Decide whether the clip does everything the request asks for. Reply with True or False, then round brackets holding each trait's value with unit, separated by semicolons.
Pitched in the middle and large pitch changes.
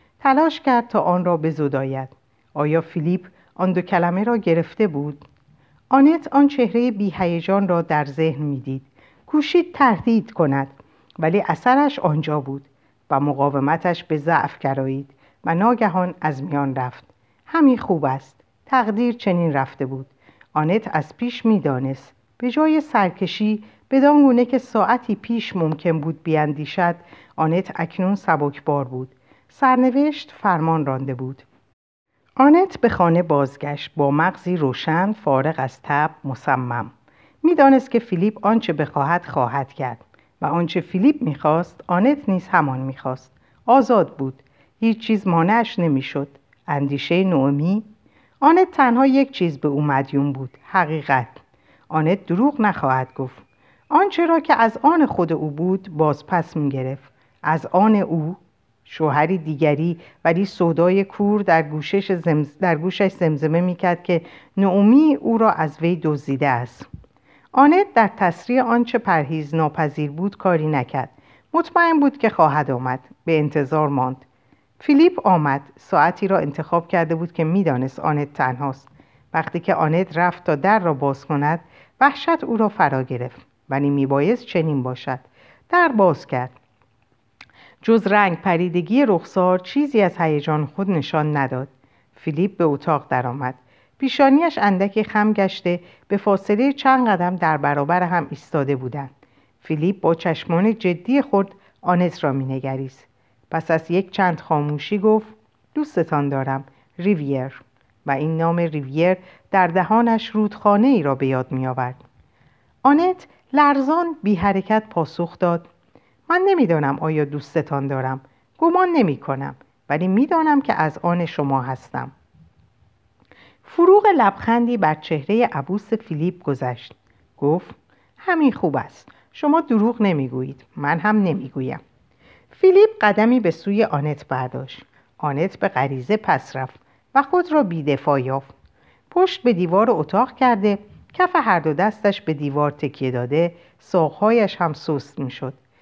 True (165 Hz; 7.2 semitones)